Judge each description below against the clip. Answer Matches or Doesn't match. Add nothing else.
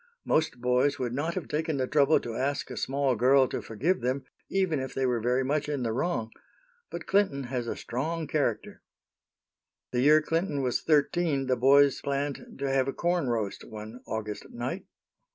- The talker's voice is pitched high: Doesn't match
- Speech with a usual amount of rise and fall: Matches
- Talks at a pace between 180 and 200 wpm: Matches